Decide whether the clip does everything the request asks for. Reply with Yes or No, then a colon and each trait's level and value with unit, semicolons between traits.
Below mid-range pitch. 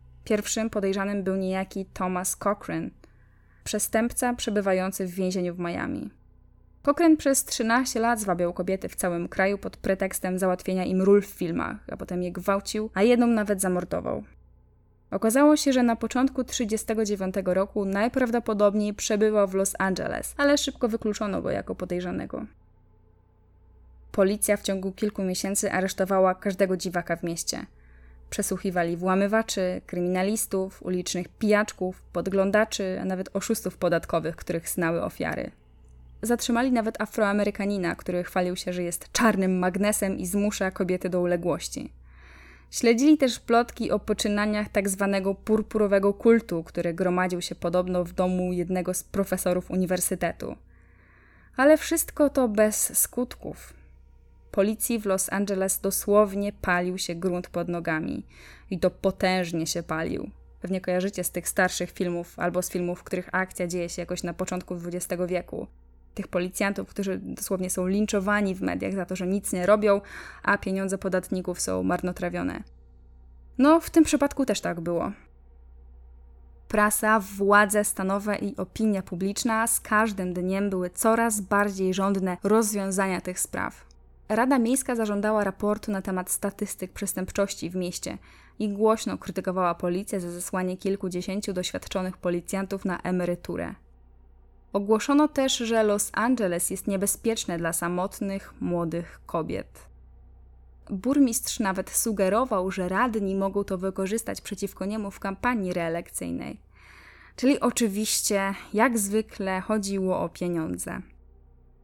No: high, 190 Hz